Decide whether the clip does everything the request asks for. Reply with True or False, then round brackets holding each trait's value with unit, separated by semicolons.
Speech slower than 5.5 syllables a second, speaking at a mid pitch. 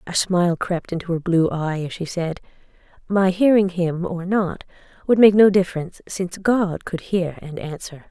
True (4.9 syllables/s; 180 Hz)